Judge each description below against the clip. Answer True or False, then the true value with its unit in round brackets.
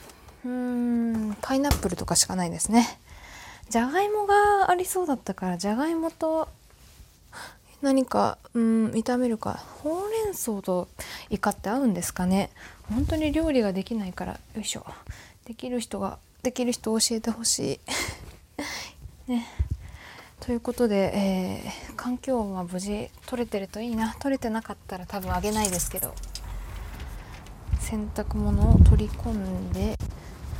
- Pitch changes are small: False (5.3 semitones)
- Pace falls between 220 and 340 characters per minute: True (285 characters per minute)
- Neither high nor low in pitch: False (225 Hz)